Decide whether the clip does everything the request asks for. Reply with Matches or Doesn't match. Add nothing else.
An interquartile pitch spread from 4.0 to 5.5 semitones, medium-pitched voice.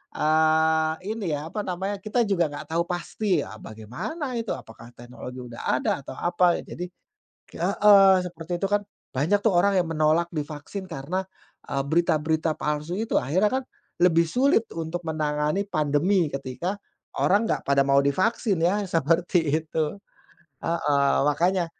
Matches